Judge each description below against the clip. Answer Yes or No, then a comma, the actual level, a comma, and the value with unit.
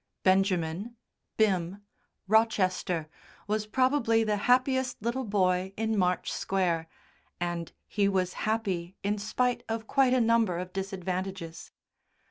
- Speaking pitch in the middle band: No, high, 200 Hz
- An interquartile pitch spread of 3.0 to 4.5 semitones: Yes, average, 3.6 semitones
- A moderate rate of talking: No, slow, 115 wpm